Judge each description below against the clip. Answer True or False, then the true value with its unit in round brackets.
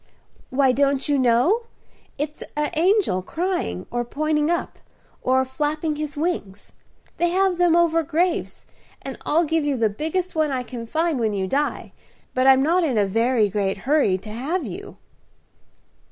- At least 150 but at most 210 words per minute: True (165 wpm)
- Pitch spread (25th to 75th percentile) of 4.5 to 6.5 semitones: True (5.4 semitones)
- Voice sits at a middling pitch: False (290 Hz)